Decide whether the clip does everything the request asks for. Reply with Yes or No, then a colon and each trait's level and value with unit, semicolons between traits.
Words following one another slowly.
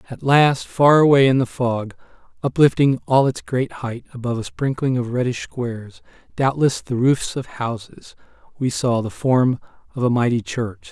No: average, 170 wpm